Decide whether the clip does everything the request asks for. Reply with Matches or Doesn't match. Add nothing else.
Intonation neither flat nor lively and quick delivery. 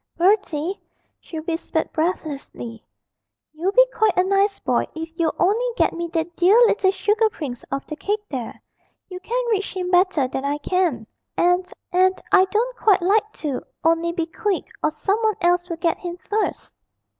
Doesn't match